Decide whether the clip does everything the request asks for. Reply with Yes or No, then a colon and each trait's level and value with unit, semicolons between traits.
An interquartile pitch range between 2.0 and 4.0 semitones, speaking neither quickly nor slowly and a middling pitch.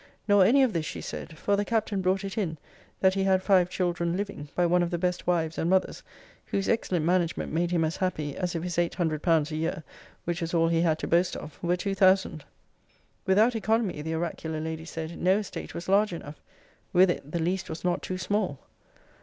No: average, 2.7 semitones; fast, 220 wpm; medium, 175 Hz